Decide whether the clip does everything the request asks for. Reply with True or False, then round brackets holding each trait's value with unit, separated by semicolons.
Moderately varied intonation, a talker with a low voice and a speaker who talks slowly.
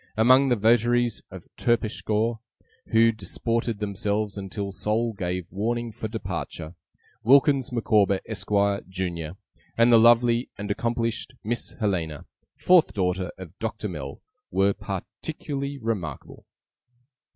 True (3.4 semitones; 110 Hz; 115 wpm)